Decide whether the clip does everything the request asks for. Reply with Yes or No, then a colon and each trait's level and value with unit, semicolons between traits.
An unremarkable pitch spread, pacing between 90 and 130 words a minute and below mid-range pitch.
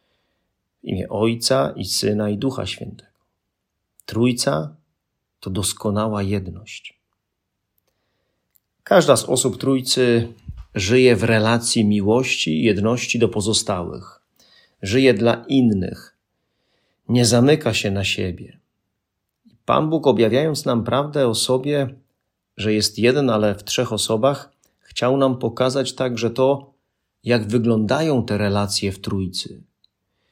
Yes: average, 3.8 semitones; slow, 110 wpm; low, 115 Hz